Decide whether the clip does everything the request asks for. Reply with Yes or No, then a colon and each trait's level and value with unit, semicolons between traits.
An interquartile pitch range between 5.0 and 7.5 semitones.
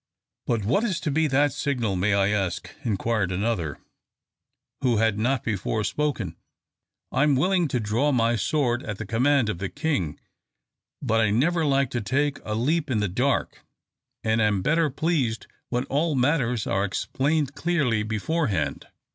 Yes: wide, 5.4 semitones